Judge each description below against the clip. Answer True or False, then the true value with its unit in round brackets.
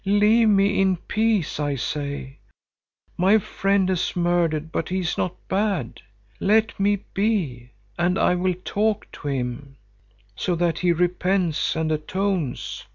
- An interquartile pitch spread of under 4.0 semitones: False (4.3 semitones)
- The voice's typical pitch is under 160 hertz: False (180 Hz)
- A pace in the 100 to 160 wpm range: True (140 wpm)